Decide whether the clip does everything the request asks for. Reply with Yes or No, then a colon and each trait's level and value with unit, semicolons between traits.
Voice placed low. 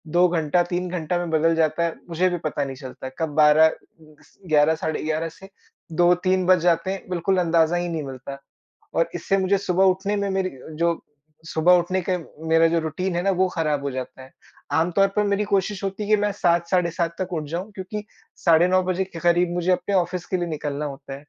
No: medium, 175 Hz